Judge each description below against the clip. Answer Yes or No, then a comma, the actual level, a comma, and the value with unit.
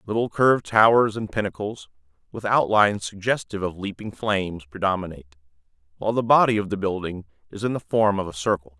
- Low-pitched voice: Yes, low, 100 Hz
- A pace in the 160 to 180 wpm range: Yes, average, 170 wpm